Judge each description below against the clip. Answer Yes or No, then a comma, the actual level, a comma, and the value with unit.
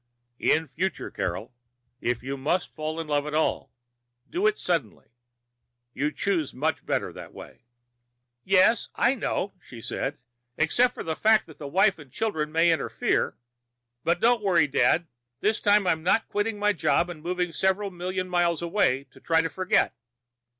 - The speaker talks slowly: No, average, 165 wpm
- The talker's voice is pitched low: No, medium, 170 Hz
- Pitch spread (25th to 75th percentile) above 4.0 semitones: Yes, average, 4.6 semitones